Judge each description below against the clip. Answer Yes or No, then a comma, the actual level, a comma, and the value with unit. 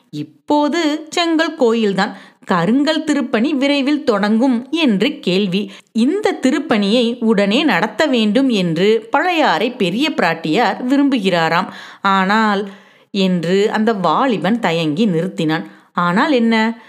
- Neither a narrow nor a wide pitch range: No, wide, 6.0 semitones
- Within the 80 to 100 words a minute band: Yes, average, 95 wpm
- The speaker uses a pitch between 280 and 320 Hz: No, high, 230 Hz